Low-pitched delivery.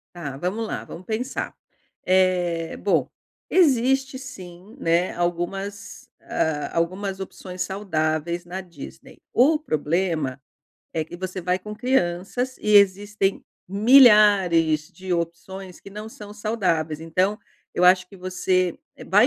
No: medium, 185 Hz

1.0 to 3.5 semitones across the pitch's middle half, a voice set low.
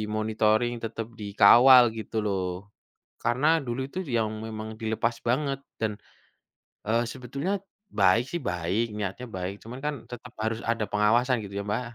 Yes: narrow, 2.6 semitones; low, 115 Hz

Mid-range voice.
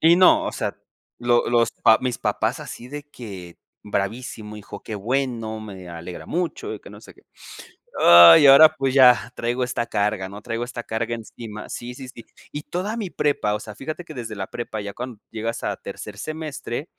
No: low, 120 Hz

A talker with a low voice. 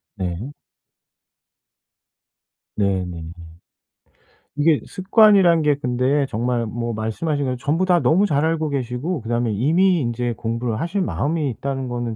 Yes: low, 130 Hz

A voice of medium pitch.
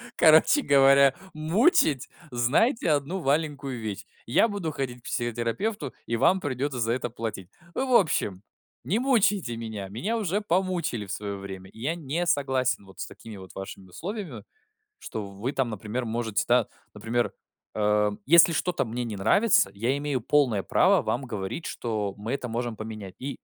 No: low, 125 Hz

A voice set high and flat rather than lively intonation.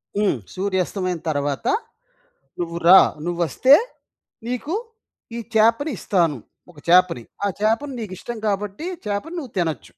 No: high, 195 Hz; average, 4.8 semitones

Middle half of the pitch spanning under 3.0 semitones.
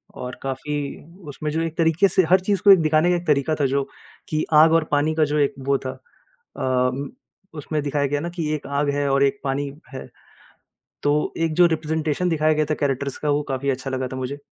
Yes: narrow, 2.5 semitones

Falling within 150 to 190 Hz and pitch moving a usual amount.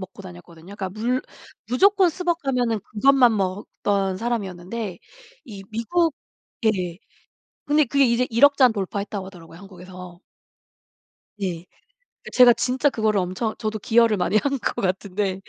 No: high, 215 Hz; average, 4.9 semitones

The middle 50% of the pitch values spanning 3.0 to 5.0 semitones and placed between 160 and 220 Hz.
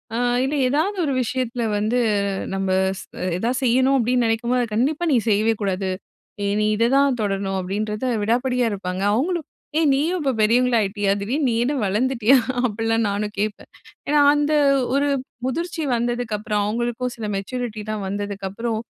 No: average, 3.8 semitones; high, 235 Hz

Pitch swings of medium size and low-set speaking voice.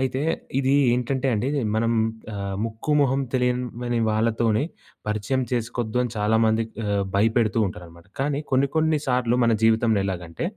Yes: average, 3.1 semitones; low, 115 Hz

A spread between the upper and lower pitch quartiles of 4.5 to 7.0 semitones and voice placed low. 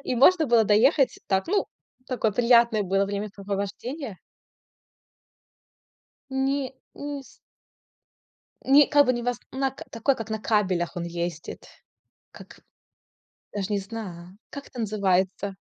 No: wide, 5.4 semitones; high, 220 Hz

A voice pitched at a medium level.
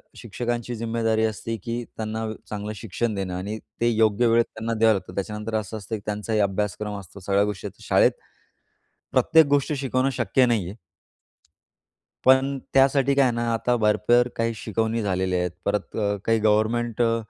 No: low, 110 Hz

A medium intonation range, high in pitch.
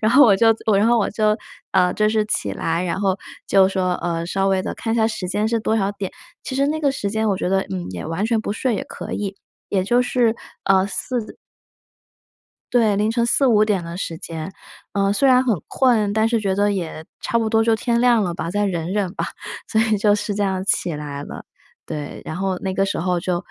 Yes: average, 3.2 semitones; high, 205 Hz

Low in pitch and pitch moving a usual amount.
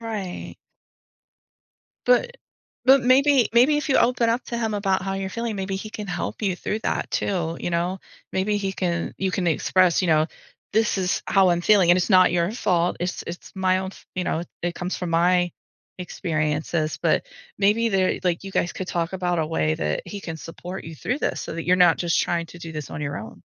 No: medium, 185 Hz; average, 3.3 semitones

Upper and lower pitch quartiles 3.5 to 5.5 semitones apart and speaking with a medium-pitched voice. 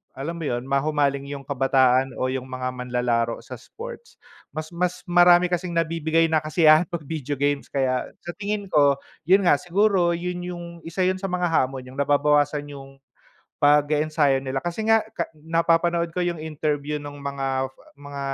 Yes: average, 4.0 semitones; medium, 150 Hz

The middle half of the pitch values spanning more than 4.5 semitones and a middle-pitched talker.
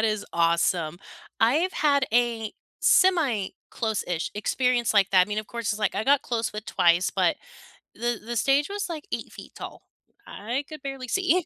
No: average, 5.2 semitones; high, 235 Hz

